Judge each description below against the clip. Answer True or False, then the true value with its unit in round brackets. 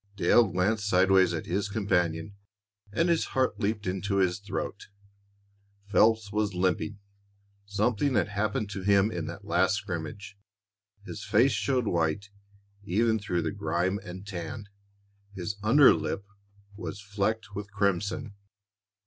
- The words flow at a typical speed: False (130 wpm)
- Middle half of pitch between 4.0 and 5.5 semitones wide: False (2.4 semitones)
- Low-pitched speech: True (100 Hz)